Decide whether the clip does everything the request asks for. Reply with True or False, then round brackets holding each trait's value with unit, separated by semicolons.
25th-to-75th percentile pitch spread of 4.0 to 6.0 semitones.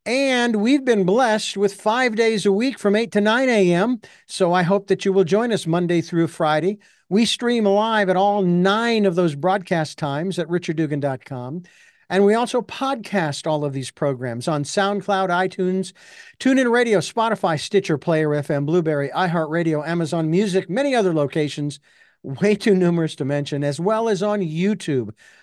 True (4.7 semitones)